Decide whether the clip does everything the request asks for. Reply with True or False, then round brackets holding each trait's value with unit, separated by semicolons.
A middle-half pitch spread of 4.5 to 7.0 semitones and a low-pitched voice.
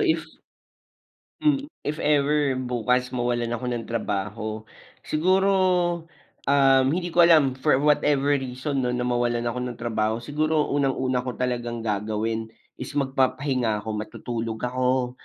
False (3.3 semitones; 125 Hz)